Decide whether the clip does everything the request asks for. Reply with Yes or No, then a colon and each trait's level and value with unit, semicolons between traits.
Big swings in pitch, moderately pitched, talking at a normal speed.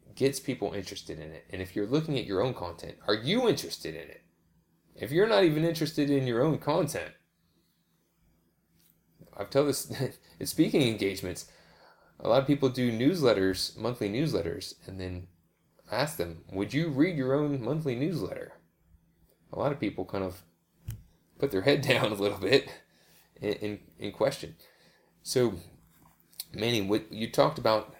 No: wide, 6.5 semitones; low, 110 Hz; average, 160 wpm